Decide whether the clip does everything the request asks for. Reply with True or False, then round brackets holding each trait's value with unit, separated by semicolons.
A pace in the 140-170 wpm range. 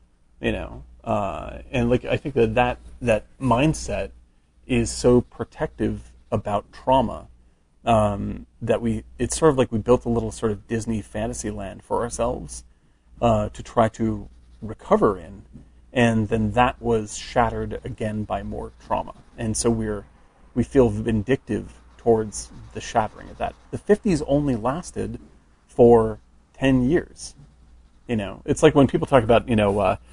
True (155 wpm)